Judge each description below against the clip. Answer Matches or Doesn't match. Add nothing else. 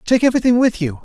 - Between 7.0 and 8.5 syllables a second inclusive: Matches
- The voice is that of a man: Matches